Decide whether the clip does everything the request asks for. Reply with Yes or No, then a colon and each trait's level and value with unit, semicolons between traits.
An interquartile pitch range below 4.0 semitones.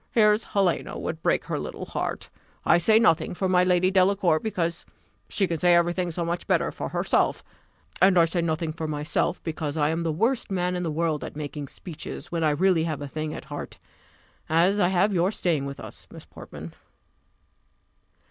Yes: average, 2.9 semitones